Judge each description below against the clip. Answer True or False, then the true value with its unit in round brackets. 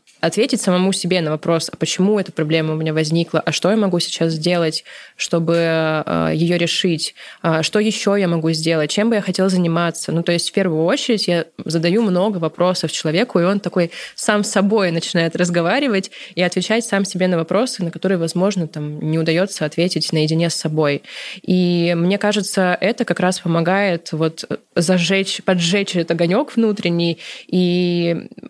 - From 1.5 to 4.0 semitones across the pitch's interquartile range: True (2.8 semitones)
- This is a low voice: False (175 Hz)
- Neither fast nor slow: False (170 wpm)